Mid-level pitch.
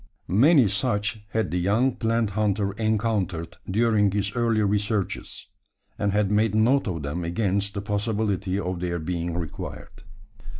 No: low, 105 Hz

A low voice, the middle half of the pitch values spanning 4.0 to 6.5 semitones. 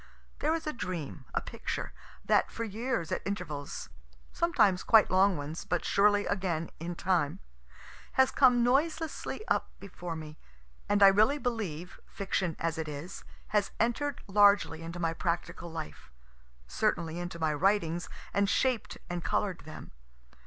No: medium, 185 Hz; average, 4.6 semitones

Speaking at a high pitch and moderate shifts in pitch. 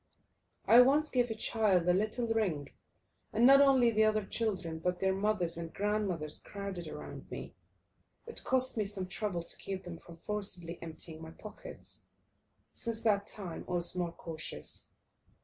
Yes: high, 200 Hz; average, 4.5 semitones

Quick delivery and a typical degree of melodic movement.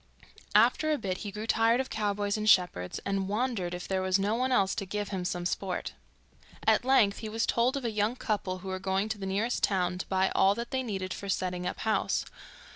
Yes: fast, 230 wpm; average, 3.1 semitones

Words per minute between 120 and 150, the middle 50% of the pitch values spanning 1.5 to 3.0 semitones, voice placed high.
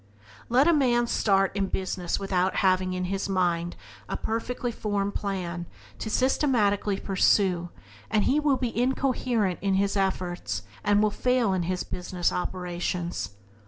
No: average, 145 wpm; average, 4.1 semitones; high, 195 Hz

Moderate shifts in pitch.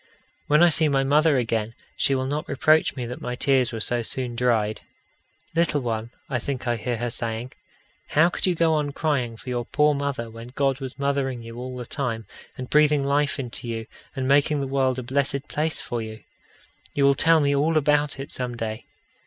Yes: average, 3.3 semitones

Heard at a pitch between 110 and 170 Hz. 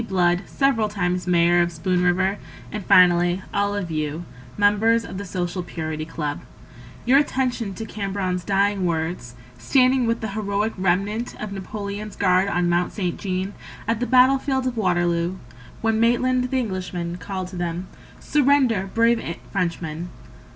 No: high, 195 Hz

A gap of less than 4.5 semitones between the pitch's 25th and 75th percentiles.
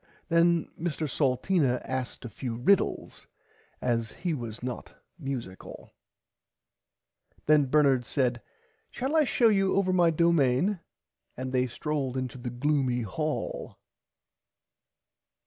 No: average, 5.2 semitones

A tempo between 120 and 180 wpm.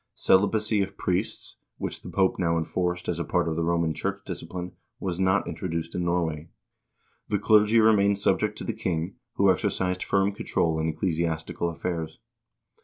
Yes: average, 165 wpm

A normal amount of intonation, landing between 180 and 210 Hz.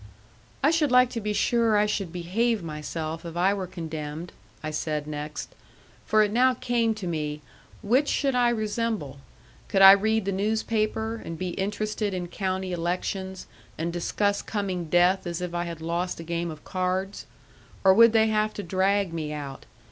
Yes: average, 4.2 semitones; high, 190 Hz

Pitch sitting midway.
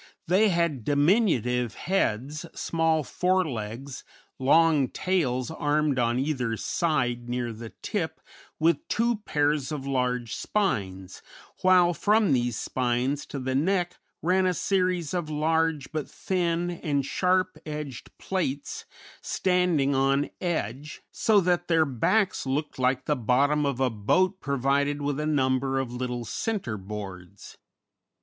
Yes: medium, 145 Hz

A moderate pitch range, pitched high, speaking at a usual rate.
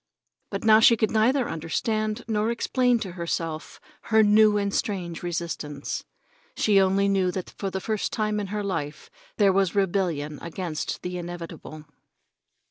Yes: average, 4.0 semitones; high, 195 Hz; average, 150 wpm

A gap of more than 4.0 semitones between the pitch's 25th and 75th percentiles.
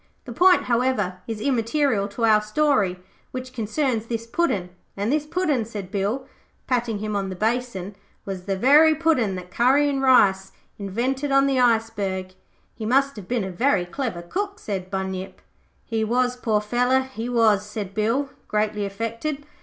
Yes: average, 4.6 semitones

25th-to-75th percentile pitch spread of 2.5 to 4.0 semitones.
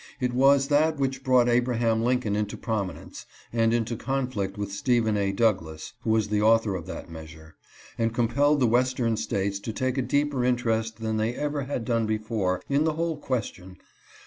Yes: average, 3.4 semitones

